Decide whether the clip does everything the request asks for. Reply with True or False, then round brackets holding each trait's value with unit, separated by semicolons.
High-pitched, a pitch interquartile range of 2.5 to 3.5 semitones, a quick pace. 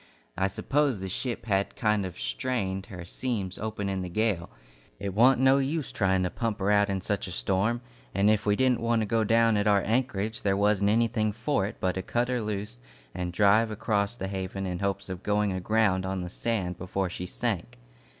False (100 Hz; 3.2 semitones; 210 wpm)